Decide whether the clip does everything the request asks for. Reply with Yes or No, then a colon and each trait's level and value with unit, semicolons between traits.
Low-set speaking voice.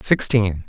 Yes: low, 105 Hz